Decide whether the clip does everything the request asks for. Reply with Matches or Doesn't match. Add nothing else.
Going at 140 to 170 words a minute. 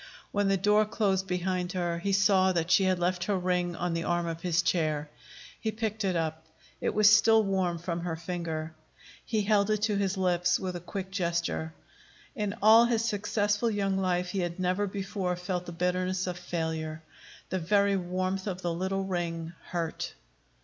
Doesn't match